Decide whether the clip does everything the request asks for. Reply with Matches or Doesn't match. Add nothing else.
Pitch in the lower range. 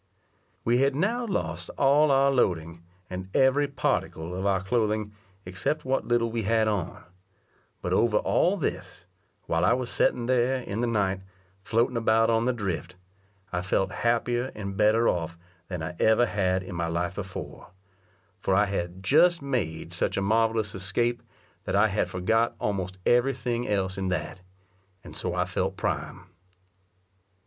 Matches